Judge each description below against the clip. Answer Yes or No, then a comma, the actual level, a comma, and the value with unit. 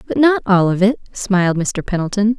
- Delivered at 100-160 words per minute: No, average, 200 wpm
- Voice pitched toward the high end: Yes, high, 205 Hz